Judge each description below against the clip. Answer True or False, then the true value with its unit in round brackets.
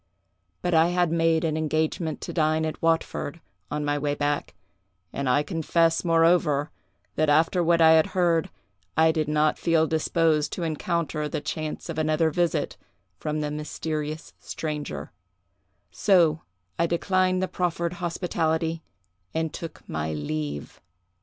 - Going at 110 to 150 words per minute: True (140 wpm)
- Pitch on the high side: False (160 Hz)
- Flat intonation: True (1.8 semitones)